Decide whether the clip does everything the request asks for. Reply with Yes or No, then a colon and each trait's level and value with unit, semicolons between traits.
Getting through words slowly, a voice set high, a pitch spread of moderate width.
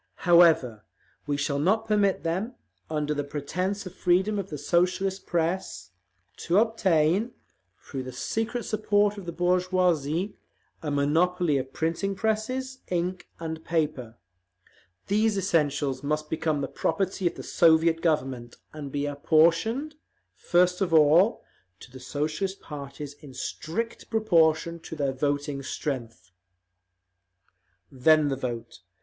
No: slow, 130 wpm; medium, 165 Hz; average, 4.8 semitones